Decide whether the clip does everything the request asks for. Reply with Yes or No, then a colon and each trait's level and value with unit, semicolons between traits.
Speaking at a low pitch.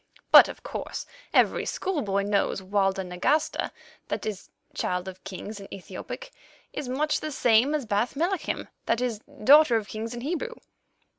No: high, 225 Hz